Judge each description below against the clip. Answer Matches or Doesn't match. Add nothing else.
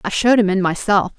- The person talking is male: Doesn't match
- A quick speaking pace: Matches